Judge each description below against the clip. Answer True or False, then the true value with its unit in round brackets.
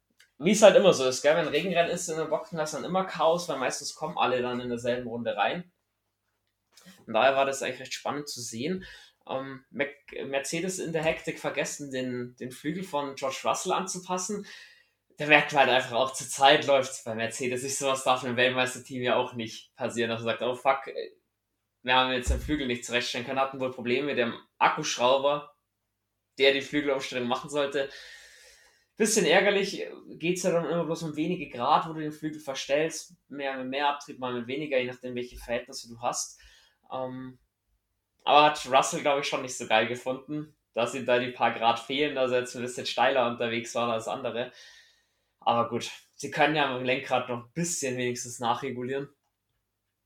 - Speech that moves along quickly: True (195 wpm)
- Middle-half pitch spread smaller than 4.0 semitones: True (3.6 semitones)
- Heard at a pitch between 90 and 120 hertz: False (135 Hz)